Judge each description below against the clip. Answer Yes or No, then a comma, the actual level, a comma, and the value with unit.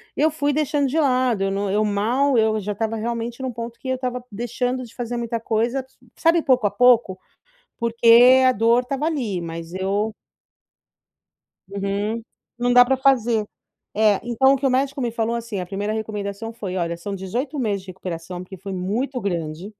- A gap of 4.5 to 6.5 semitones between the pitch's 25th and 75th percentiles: No, average, 4.0 semitones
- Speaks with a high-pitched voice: Yes, high, 230 Hz